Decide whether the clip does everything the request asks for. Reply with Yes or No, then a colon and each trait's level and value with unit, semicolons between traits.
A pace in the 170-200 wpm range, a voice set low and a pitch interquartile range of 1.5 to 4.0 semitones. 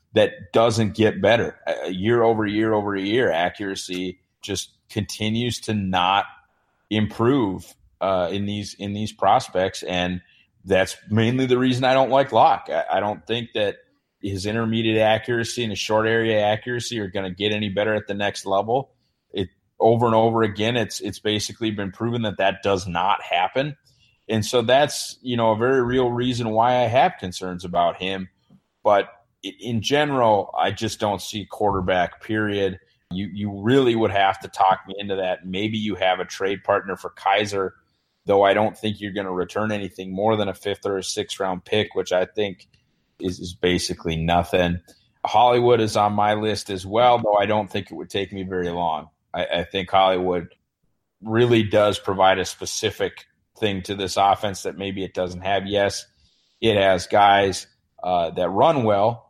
Yes: average, 180 wpm; low, 105 Hz; average, 2.8 semitones